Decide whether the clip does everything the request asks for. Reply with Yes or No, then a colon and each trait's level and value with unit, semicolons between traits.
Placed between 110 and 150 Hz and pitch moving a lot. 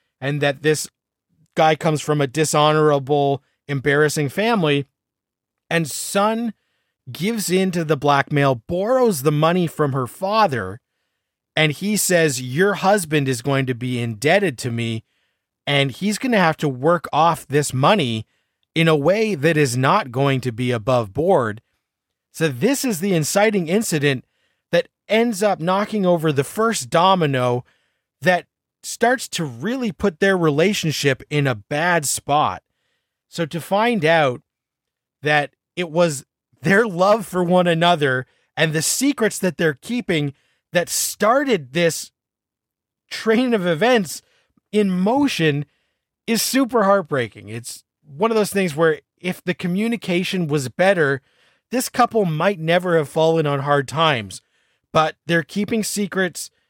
No: medium, 165 Hz; wide, 5.7 semitones